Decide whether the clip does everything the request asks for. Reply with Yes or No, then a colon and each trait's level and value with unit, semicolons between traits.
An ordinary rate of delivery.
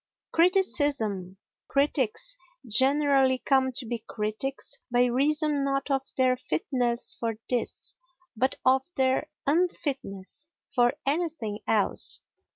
No: slow, 105 wpm